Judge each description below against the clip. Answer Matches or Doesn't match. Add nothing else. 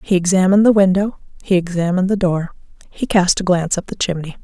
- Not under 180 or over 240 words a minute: Matches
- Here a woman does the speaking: Matches